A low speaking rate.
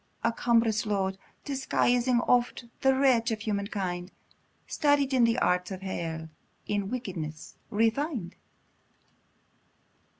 Yes: slow, 105 wpm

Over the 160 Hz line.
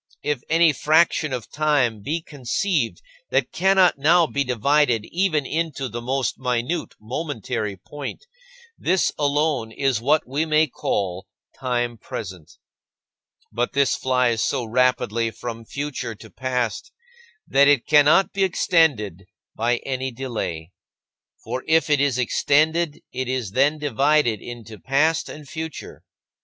No: low, 135 Hz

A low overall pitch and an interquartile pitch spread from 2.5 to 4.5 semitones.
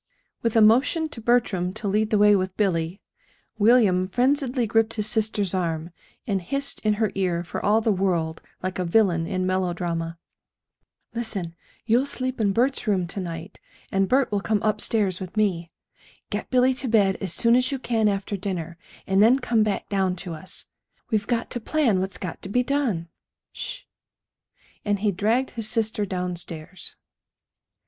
No: high, 205 Hz; average, 3.9 semitones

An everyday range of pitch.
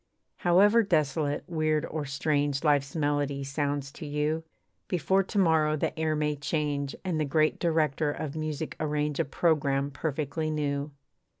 No: narrow, 1.8 semitones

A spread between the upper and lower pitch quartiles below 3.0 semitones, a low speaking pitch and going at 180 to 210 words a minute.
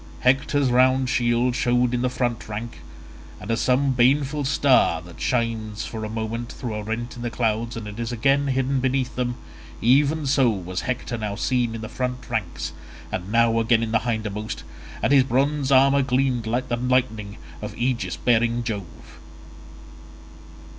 No: narrow, 2.6 semitones; low, 120 Hz; average, 165 wpm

